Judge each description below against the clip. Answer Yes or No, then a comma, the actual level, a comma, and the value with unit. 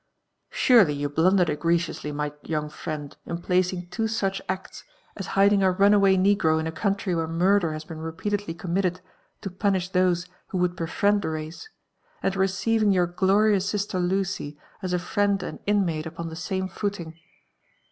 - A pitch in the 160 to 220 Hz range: Yes, medium, 185 Hz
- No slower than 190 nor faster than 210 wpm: No, average, 165 wpm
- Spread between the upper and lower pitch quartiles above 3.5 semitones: No, average, 3.2 semitones